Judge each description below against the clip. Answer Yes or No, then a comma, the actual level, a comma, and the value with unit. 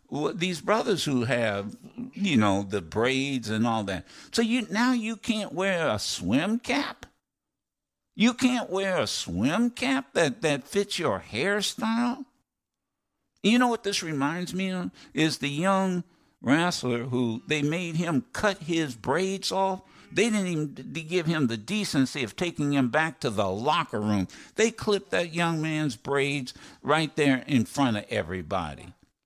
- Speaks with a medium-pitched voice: Yes, medium, 170 Hz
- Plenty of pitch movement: Yes, wide, 7.8 semitones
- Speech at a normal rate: Yes, average, 160 wpm